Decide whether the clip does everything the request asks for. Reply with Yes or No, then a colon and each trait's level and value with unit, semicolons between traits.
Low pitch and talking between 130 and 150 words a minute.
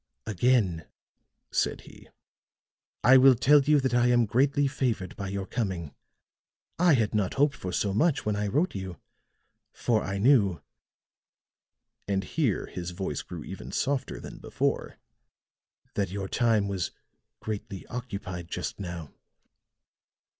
Yes: low, 105 Hz; slow, 135 wpm